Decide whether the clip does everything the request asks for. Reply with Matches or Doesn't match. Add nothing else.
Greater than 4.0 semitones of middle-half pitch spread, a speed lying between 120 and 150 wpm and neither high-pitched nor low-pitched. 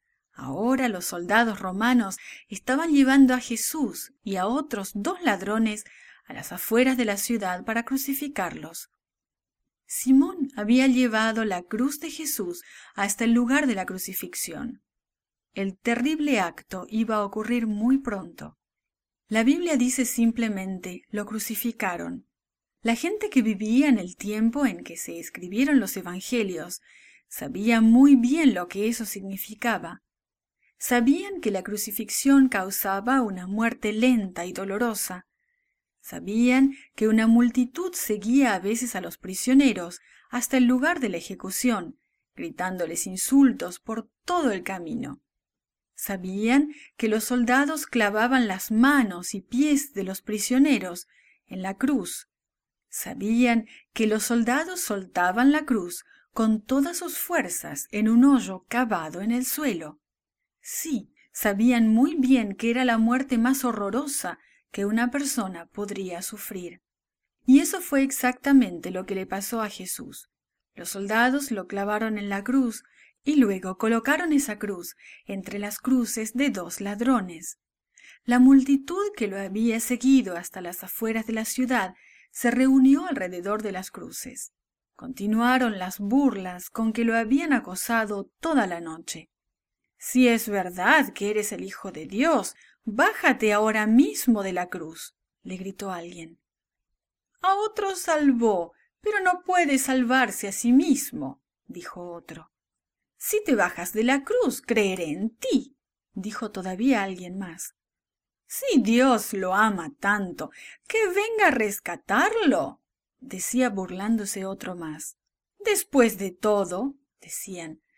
Doesn't match